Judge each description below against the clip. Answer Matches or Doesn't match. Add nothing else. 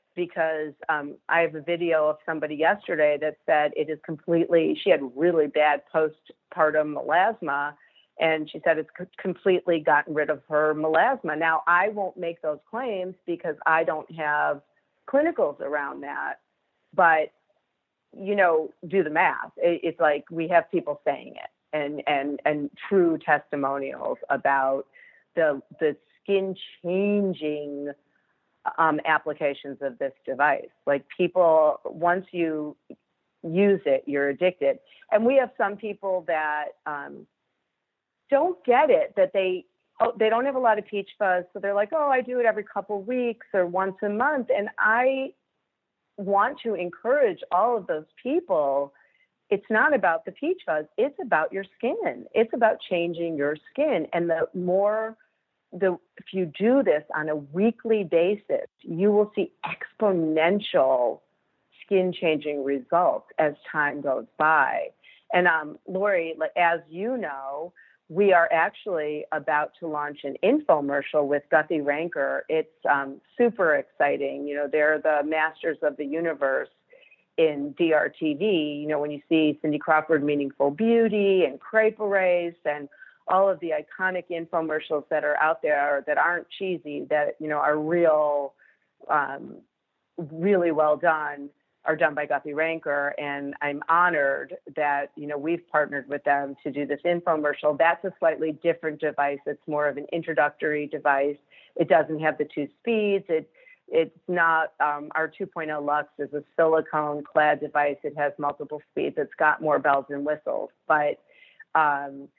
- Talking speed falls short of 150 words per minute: Doesn't match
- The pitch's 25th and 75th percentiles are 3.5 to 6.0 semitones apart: Matches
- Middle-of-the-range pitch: Matches